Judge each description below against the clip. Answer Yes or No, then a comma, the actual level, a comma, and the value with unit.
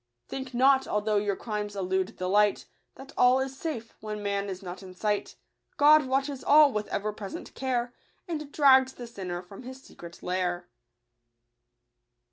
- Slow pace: No, average, 160 wpm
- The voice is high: Yes, high, 215 Hz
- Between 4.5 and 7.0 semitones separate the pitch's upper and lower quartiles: Yes, average, 5.1 semitones